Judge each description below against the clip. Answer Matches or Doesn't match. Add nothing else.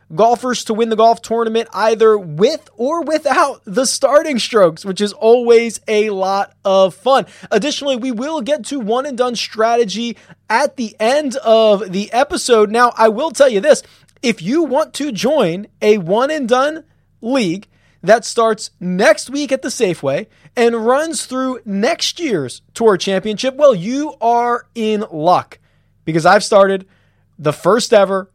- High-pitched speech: Matches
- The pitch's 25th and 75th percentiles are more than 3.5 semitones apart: Matches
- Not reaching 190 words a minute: Matches